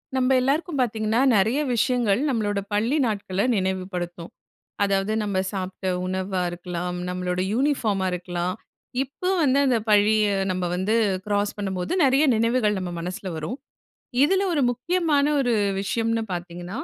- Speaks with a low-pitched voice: No, high, 205 Hz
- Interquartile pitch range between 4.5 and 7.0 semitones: Yes, average, 4.9 semitones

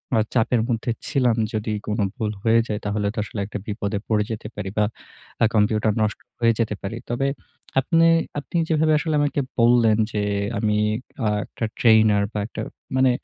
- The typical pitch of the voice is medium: No, low, 110 Hz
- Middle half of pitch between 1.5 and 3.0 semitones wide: Yes, narrow, 2.6 semitones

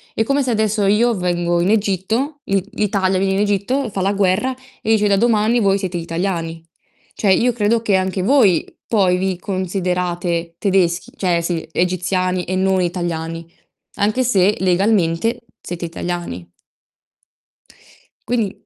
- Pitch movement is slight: No, average, 3.2 semitones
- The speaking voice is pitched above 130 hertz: Yes, high, 190 Hz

